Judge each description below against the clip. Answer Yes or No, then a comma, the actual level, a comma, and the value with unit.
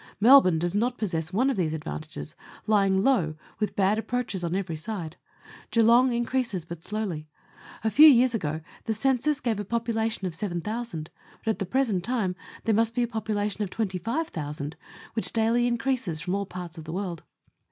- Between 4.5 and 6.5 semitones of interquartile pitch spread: Yes, average, 5.1 semitones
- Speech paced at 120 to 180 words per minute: No, average, 190 wpm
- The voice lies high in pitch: Yes, high, 210 Hz